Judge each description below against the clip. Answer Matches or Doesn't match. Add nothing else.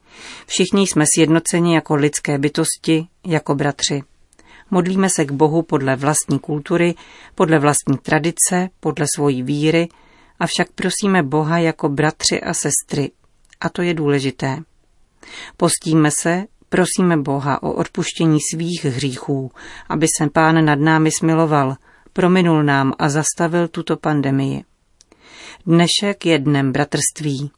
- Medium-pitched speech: Matches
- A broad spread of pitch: Doesn't match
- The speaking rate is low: Doesn't match